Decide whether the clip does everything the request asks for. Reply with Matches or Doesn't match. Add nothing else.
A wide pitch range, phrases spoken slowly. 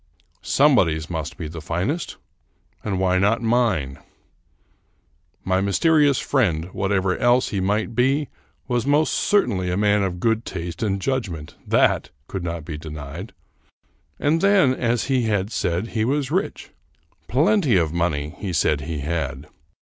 Doesn't match